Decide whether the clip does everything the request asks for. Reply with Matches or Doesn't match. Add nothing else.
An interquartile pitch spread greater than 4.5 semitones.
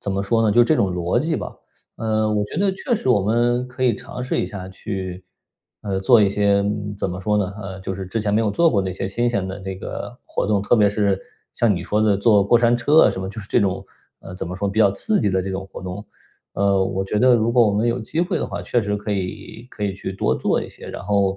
Doesn't match